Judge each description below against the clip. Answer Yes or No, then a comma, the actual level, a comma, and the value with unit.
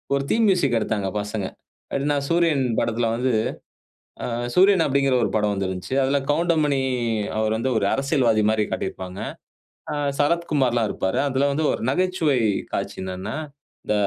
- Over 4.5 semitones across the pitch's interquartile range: Yes, wide, 5.5 semitones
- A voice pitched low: Yes, low, 130 Hz